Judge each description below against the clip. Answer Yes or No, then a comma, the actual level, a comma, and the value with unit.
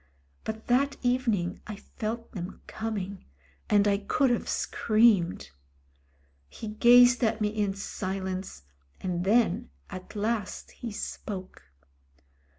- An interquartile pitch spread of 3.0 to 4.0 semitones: Yes, average, 3.5 semitones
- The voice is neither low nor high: No, high, 210 Hz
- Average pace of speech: No, slow, 115 wpm